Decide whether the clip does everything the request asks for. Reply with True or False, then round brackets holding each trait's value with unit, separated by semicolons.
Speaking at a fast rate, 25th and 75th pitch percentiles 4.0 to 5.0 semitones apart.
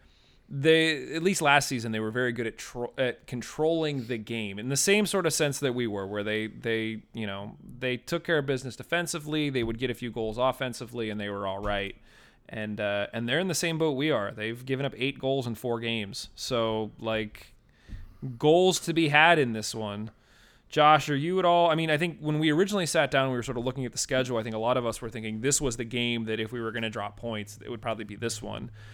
True (255 wpm; 4.7 semitones)